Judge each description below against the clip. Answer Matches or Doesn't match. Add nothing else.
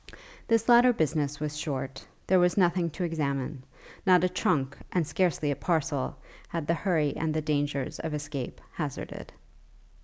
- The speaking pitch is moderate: Matches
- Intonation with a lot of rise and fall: Doesn't match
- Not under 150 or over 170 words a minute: Matches